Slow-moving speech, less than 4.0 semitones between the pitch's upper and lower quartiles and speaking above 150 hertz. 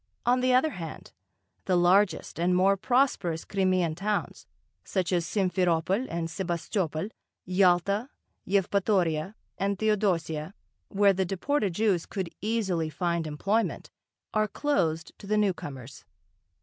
Yes: slow, 120 wpm; average, 3.4 semitones; high, 190 Hz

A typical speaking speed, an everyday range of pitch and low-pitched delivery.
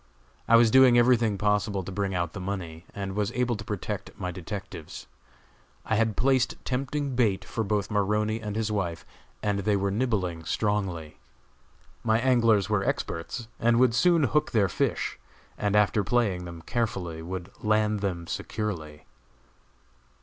Yes: average, 155 wpm; average, 3.4 semitones; low, 105 Hz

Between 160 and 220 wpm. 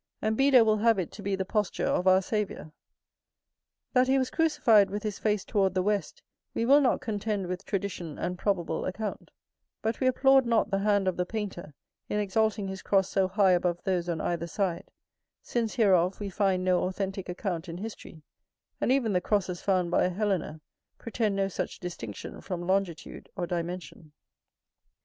Yes: average, 180 wpm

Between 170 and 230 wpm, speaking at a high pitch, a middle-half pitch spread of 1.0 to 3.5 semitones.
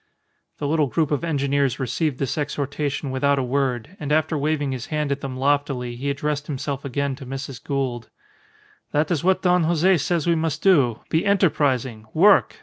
No: average, 180 wpm; medium, 140 Hz; average, 2.8 semitones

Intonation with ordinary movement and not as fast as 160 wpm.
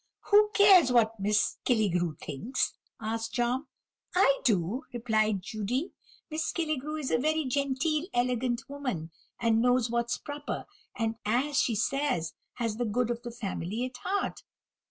Yes: average, 4.3 semitones; average, 145 wpm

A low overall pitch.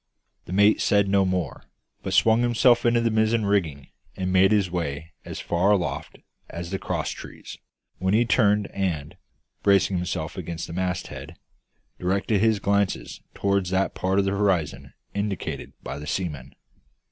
Yes: very low, 95 Hz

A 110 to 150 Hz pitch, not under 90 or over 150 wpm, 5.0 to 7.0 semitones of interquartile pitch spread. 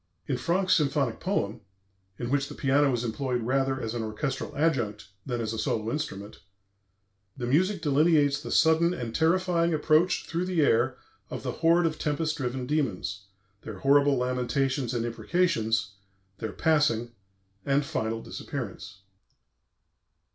Yes: low, 135 Hz; average, 140 wpm; average, 5.3 semitones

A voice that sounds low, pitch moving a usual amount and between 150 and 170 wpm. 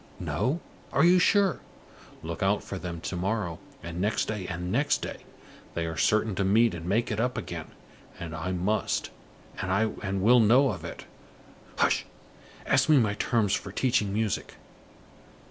Yes: low, 105 Hz; average, 4.4 semitones; average, 160 wpm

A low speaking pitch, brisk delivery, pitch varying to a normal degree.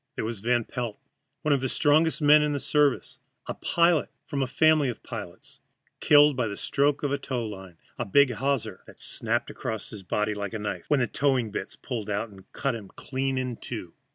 Yes: low, 130 Hz; fast, 210 wpm; average, 4.9 semitones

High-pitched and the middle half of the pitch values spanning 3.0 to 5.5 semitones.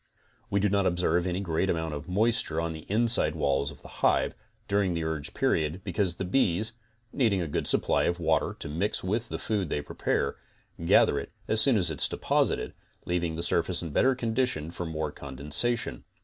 No: very low, 85 Hz; average, 4.3 semitones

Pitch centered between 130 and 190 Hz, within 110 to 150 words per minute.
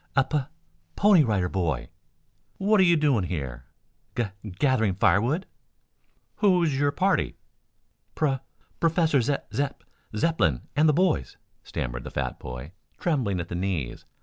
Yes: low, 135 Hz; average, 140 wpm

